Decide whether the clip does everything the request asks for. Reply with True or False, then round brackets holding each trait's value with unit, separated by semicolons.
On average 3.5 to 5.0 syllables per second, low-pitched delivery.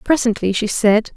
False (4.9 syllables/s; 225 Hz)